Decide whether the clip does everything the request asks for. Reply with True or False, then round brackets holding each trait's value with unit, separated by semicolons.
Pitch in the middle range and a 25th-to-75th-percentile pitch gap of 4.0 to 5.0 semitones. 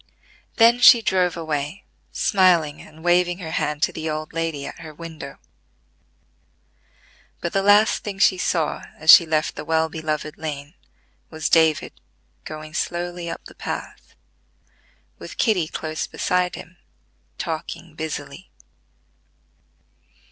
False (160 Hz; 2.4 semitones)